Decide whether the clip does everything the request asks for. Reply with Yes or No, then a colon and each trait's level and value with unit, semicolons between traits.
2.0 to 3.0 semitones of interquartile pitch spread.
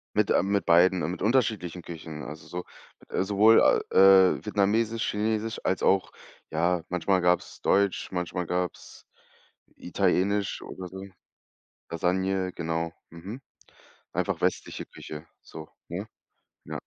Yes: average, 2.7 semitones